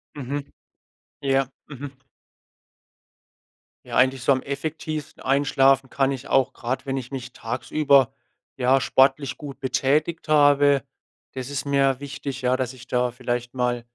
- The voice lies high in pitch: No, low, 135 Hz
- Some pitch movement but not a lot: No, narrow, 1.7 semitones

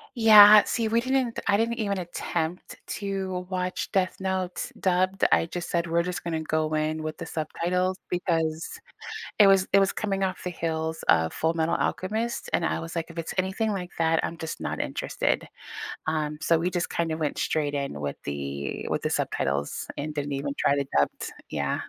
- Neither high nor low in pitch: Yes, medium, 170 Hz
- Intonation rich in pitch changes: No, average, 3.3 semitones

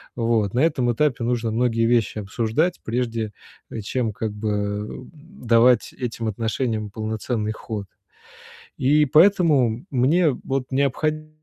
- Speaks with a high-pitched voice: No, low, 120 Hz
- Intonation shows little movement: No, average, 3.4 semitones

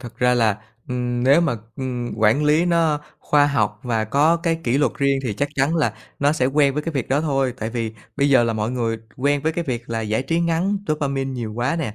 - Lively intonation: No, average, 3.9 semitones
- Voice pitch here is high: No, low, 135 Hz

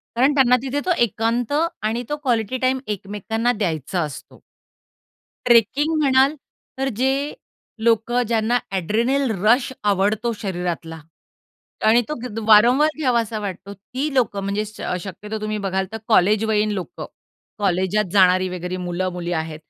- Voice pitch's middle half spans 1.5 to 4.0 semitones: No, average, 4.4 semitones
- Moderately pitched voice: No, high, 215 Hz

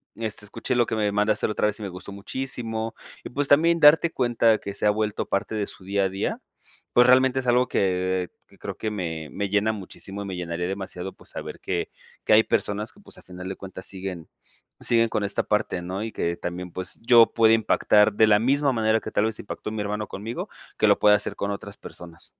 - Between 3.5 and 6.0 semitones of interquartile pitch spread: No, average, 2.9 semitones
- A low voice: Yes, low, 105 Hz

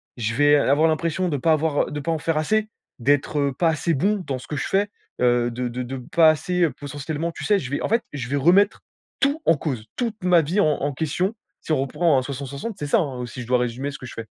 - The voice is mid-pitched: Yes, medium, 145 Hz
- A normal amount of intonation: Yes, average, 4.3 semitones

